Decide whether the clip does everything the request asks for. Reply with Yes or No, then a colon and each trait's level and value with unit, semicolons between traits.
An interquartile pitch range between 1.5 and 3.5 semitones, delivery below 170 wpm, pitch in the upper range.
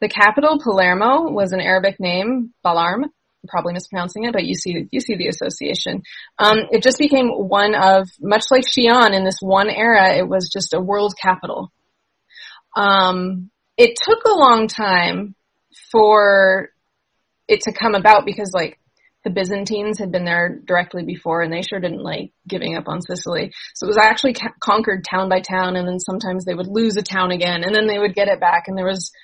No: average, 2.9 semitones; average, 190 wpm; high, 200 Hz